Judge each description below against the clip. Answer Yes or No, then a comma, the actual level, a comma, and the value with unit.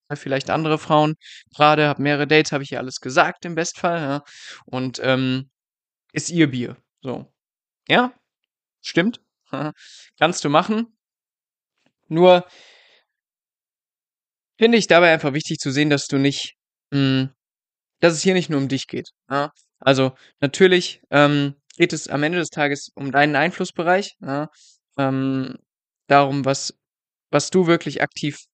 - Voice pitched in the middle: Yes, medium, 150 Hz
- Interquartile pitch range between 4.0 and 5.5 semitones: No, average, 3.6 semitones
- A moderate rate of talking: Yes, average, 140 wpm